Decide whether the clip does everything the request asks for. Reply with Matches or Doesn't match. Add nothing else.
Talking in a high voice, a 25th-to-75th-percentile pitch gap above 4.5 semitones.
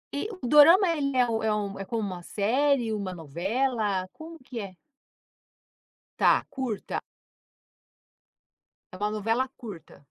Matches